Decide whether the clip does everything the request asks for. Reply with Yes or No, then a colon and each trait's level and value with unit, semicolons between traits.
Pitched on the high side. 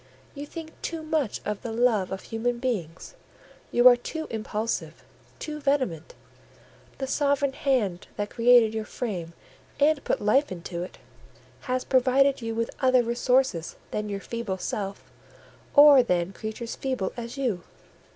Yes: high, 235 Hz